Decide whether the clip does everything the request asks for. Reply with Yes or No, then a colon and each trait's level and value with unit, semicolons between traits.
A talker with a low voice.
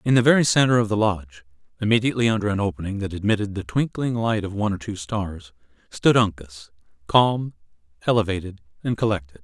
Yes: low, 100 Hz